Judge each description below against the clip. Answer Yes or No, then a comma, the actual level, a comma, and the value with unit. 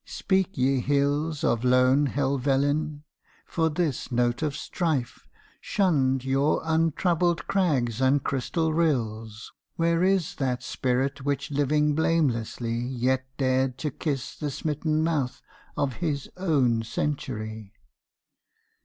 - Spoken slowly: Yes, slow, 115 wpm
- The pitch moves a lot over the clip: No, average, 3.7 semitones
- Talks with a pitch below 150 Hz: Yes, medium, 140 Hz